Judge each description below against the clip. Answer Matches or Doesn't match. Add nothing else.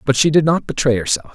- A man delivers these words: Matches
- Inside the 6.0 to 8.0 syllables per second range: Matches